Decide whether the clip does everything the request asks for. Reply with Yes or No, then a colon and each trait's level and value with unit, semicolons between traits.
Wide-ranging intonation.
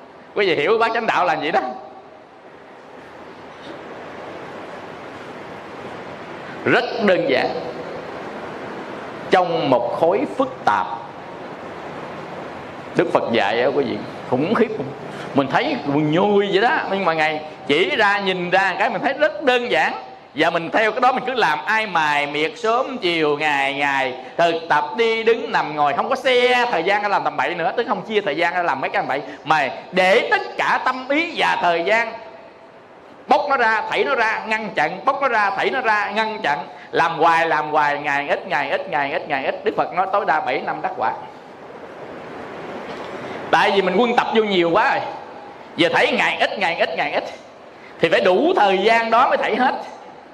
Yes: wide, 6.1 semitones